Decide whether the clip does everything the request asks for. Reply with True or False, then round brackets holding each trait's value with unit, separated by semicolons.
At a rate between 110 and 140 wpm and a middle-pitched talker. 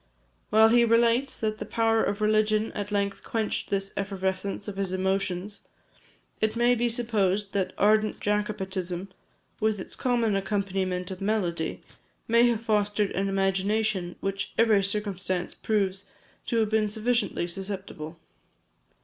False (135 wpm; 205 Hz)